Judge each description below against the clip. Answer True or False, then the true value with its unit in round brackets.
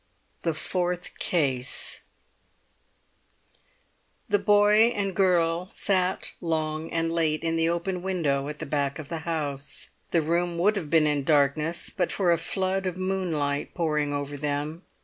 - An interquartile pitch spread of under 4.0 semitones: True (3.3 semitones)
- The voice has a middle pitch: True (165 Hz)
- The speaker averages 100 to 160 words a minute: True (150 wpm)